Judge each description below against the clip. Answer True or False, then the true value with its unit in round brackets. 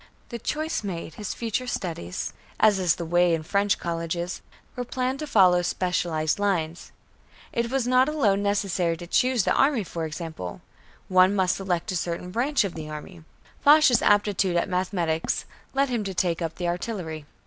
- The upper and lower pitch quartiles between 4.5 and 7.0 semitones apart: True (4.9 semitones)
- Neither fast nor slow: True (170 wpm)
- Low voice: False (185 Hz)